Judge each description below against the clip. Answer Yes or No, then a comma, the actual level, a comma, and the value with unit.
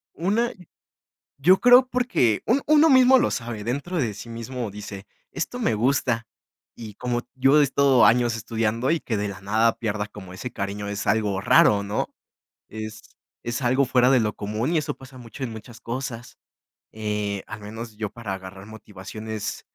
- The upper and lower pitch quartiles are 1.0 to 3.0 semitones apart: No, average, 4.0 semitones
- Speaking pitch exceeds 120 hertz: No, low, 115 Hz